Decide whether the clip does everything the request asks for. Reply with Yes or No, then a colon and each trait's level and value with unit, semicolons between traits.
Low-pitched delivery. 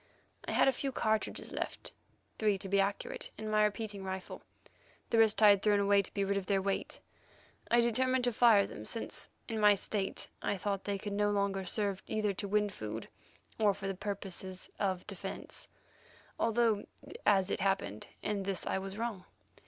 No: high, 200 Hz